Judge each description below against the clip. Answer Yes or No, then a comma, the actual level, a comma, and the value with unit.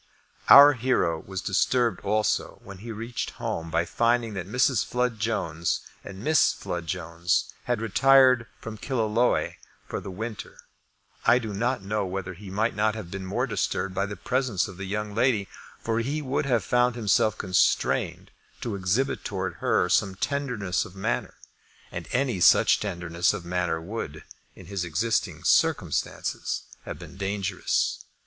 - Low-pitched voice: Yes, low, 105 Hz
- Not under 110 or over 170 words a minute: Yes, average, 155 wpm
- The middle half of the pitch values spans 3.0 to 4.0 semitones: No, average, 4.4 semitones